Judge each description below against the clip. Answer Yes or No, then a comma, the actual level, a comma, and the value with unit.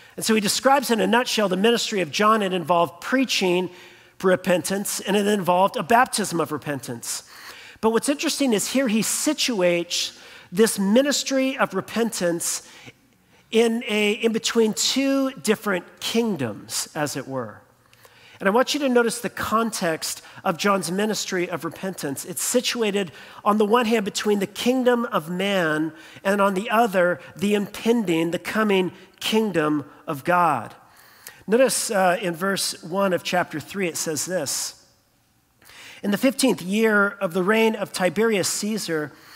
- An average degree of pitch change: Yes, average, 4.4 semitones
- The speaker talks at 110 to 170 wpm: Yes, average, 150 wpm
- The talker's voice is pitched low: No, high, 200 Hz